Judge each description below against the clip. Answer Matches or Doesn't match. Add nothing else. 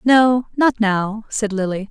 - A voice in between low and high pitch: Doesn't match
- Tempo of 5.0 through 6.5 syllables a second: Doesn't match